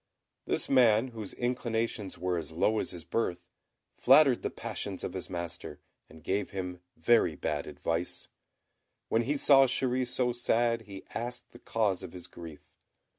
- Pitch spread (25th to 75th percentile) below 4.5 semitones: No, wide, 5.6 semitones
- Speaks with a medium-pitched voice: No, low, 110 Hz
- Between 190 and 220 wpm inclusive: No, average, 160 wpm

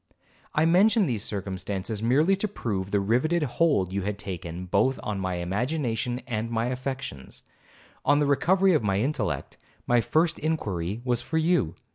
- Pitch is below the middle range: Yes, low, 120 Hz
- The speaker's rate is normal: Yes, average, 160 wpm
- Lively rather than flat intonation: Yes, wide, 7.6 semitones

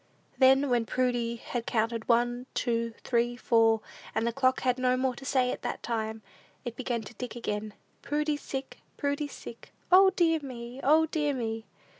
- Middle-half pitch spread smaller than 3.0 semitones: Yes, narrow, 2.6 semitones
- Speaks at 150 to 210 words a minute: Yes, average, 175 wpm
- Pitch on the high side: Yes, high, 245 Hz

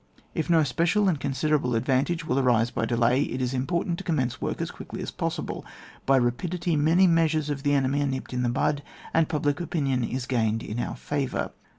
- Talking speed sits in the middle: No, fast, 210 wpm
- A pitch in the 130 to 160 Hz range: Yes, medium, 140 Hz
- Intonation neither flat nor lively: Yes, average, 4.2 semitones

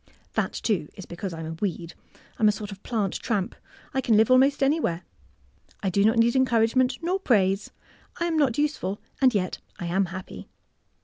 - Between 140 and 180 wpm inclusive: No, average, 195 wpm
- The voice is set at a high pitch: Yes, high, 215 Hz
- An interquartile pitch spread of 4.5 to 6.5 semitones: Yes, wide, 5.4 semitones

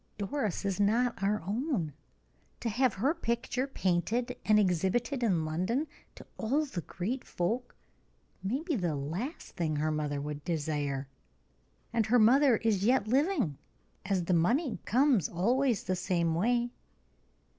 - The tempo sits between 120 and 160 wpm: Yes, average, 145 wpm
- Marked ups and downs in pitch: Yes, wide, 6.2 semitones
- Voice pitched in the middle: No, high, 210 Hz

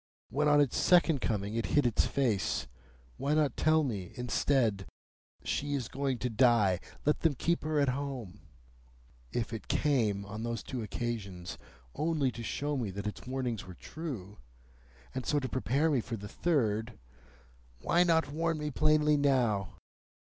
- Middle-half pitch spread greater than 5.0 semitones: Yes, wide, 5.4 semitones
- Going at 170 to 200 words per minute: No, average, 160 wpm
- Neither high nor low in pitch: No, low, 130 Hz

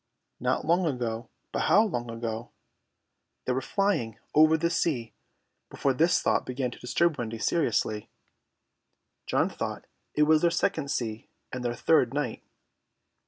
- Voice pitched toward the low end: Yes, low, 130 Hz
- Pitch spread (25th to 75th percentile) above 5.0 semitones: Yes, wide, 5.4 semitones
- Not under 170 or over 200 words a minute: No, average, 145 wpm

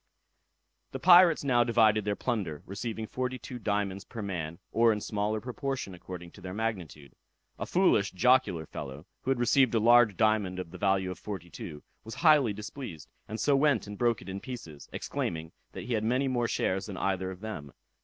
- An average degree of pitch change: Yes, average, 4.6 semitones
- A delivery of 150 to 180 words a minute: No, average, 195 wpm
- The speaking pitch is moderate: No, low, 105 Hz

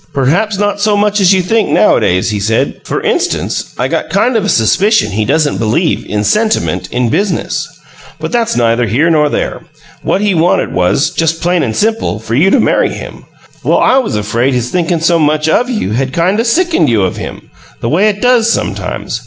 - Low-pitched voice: No, medium, 170 Hz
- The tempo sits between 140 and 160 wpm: No, fast, 205 wpm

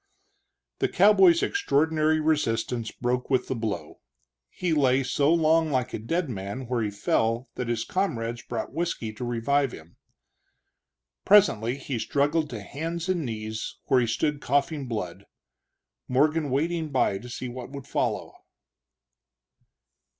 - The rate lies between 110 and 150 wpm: Yes, average, 140 wpm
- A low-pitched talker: Yes, low, 130 Hz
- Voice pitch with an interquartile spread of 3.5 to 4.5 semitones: No, average, 5.2 semitones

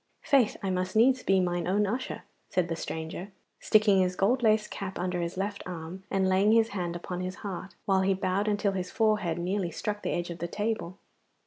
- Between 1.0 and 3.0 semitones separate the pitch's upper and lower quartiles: Yes, average, 2.7 semitones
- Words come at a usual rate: No, fast, 210 wpm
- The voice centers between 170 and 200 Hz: Yes, high, 190 Hz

